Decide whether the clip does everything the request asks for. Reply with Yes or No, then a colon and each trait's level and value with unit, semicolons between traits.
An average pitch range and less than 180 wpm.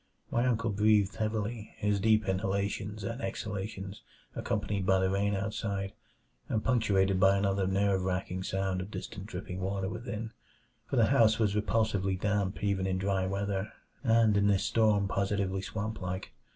No: narrow, 2.0 semitones; average, 155 wpm